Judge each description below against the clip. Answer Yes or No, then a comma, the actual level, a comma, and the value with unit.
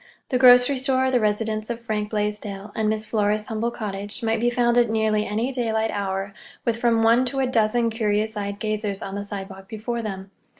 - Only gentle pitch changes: Yes, narrow, 2.2 semitones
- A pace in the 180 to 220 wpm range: Yes, average, 200 wpm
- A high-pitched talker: Yes, high, 220 Hz